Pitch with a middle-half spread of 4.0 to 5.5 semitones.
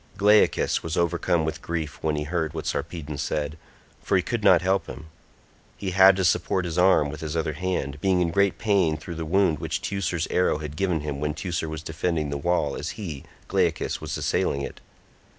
No: average, 3.4 semitones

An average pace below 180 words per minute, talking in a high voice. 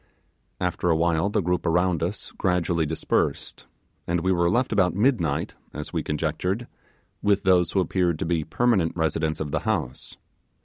No: average, 165 wpm; very low, 90 Hz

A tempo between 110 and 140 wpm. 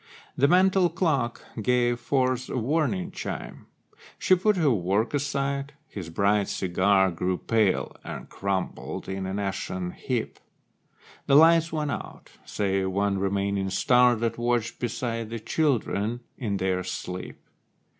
Yes: slow, 135 wpm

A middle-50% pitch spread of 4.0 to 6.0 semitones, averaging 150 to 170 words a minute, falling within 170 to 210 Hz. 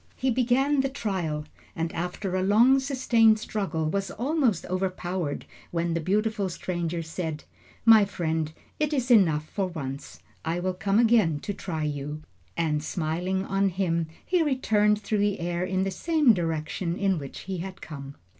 Yes: average, 4.8 semitones; average, 165 wpm; medium, 185 Hz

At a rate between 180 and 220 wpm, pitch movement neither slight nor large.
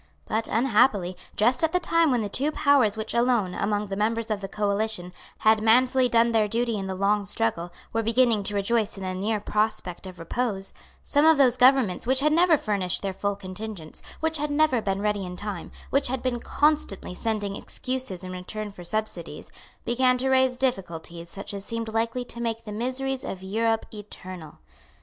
Yes: average, 190 wpm; average, 4.3 semitones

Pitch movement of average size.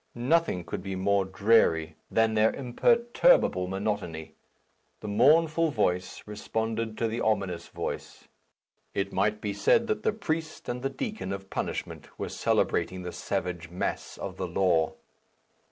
No: wide, 5.8 semitones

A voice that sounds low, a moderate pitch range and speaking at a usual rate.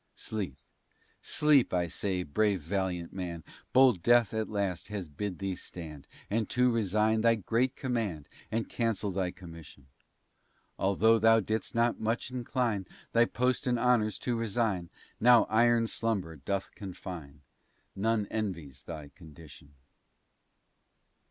No: low, 105 Hz; average, 4.5 semitones; slow, 130 wpm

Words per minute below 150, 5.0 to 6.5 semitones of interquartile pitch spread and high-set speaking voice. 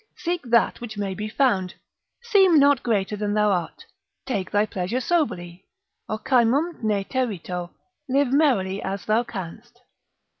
Yes: average, 140 wpm; wide, 5.4 semitones; high, 215 Hz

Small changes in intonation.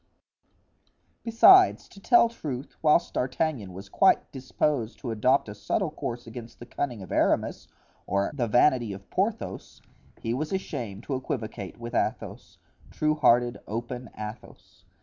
No: average, 5.1 semitones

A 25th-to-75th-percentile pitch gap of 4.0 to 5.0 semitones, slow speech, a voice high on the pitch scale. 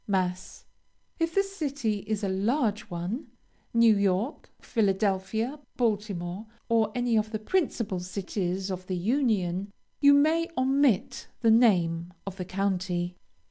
Yes: average, 4.7 semitones; slow, 130 wpm; high, 210 Hz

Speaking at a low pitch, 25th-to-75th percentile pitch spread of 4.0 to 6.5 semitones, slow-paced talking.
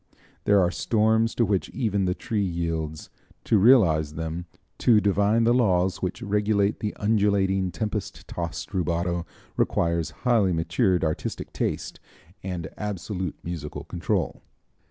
No: very low, 95 Hz; average, 3.6 semitones; slow, 130 wpm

